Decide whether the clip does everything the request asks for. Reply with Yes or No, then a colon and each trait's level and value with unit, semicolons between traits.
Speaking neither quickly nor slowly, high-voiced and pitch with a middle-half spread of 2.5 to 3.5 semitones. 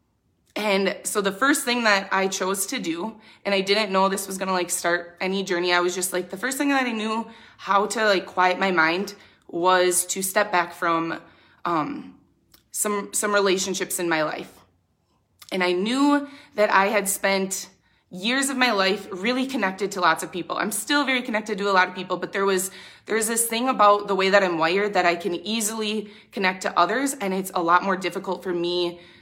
No: fast, 210 wpm; high, 195 Hz; average, 2.8 semitones